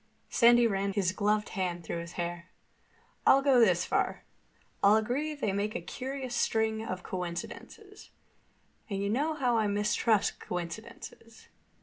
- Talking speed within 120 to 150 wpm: Yes, average, 140 wpm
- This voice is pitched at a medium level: No, high, 215 Hz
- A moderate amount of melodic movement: Yes, average, 4.4 semitones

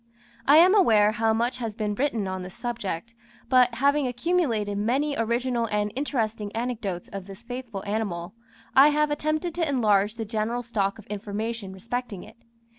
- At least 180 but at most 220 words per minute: No, average, 165 wpm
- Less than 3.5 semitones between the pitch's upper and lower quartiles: No, average, 3.8 semitones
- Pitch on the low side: No, high, 230 Hz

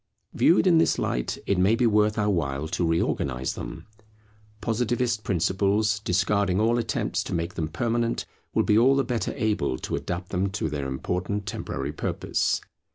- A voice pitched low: Yes, low, 100 Hz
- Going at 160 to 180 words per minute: Yes, average, 165 wpm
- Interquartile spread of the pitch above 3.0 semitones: Yes, average, 5.1 semitones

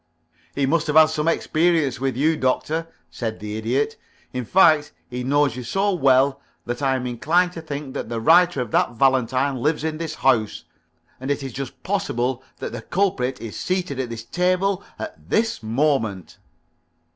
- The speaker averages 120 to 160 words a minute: No, average, 180 wpm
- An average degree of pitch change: Yes, average, 4.7 semitones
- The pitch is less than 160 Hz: Yes, medium, 140 Hz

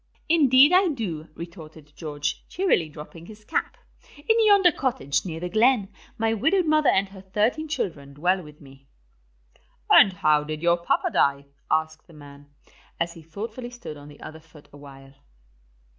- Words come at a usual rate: Yes, average, 160 wpm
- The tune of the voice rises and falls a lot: Yes, wide, 8.2 semitones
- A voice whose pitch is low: No, medium, 170 Hz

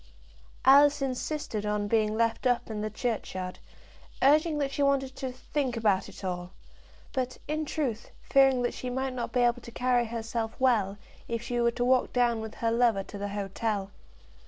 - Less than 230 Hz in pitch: No, high, 240 Hz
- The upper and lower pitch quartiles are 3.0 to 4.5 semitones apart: Yes, average, 3.3 semitones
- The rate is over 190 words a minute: No, average, 180 wpm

